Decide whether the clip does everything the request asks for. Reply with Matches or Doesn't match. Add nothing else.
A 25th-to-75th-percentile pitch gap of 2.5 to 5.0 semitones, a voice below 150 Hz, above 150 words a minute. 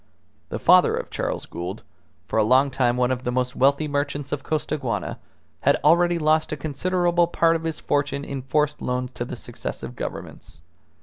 Matches